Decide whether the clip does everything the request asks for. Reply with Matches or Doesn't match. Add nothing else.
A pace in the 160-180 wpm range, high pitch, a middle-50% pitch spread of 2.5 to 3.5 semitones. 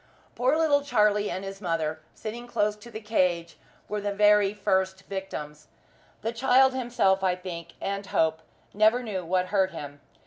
Matches